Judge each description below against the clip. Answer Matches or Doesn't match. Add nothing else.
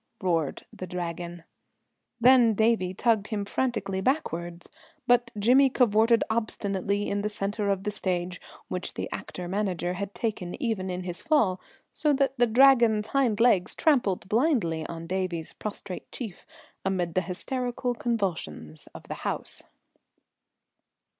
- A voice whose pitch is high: Matches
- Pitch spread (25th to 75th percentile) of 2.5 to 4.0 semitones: Doesn't match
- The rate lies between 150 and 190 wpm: Doesn't match